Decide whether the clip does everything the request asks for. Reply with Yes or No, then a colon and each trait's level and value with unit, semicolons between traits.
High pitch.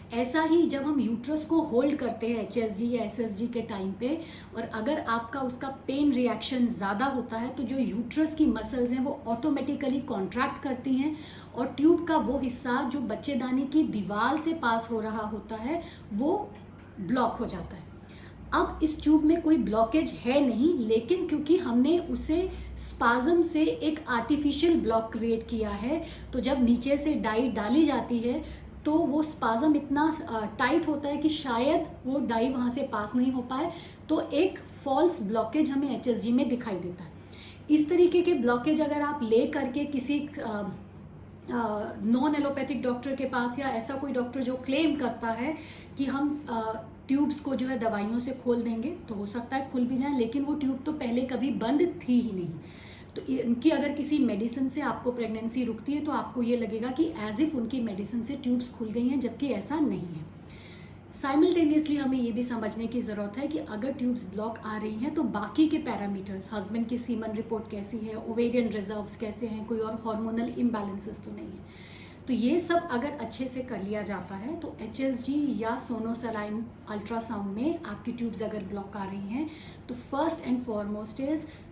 Yes: very high, 250 Hz